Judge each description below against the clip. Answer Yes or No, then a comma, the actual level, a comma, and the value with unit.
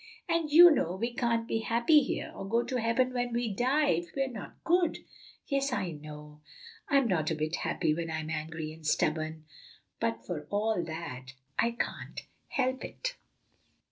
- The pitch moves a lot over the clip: Yes, wide, 8.3 semitones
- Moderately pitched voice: No, high, 215 Hz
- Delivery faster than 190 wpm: No, average, 180 wpm